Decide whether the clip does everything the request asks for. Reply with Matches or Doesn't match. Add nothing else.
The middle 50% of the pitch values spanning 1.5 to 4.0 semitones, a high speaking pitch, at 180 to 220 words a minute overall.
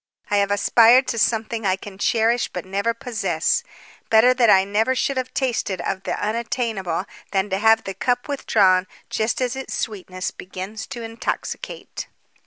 Doesn't match